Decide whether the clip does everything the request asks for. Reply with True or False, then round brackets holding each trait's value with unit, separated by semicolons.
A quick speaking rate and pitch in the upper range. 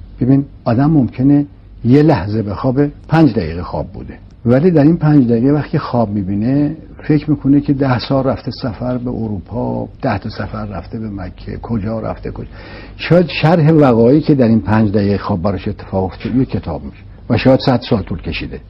False (185 wpm; 115 Hz)